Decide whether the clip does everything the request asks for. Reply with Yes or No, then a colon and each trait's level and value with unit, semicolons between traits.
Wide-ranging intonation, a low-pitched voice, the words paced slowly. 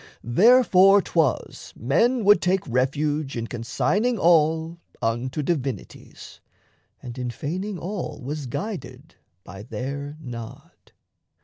No: wide, 6.8 semitones; medium, 150 Hz; slow, 105 wpm